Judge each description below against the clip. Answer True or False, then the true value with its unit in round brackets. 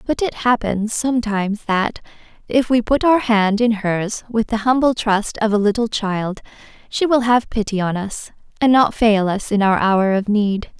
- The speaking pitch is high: True (220 Hz)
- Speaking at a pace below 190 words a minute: False (195 wpm)